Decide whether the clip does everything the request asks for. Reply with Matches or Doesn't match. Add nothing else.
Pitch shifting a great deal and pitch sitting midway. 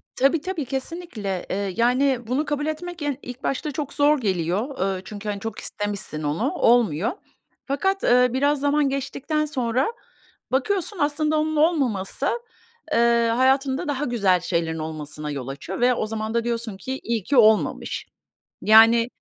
Doesn't match